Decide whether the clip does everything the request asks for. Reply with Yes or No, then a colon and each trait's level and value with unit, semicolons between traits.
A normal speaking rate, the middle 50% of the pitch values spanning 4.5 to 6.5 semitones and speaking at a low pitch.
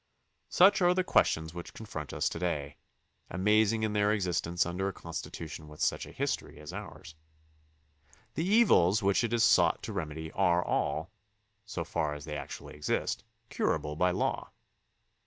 Yes: average, 160 wpm; average, 5.2 semitones; very low, 90 Hz